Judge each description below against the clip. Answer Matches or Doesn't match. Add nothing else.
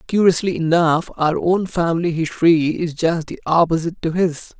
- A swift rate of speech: Doesn't match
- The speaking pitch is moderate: Matches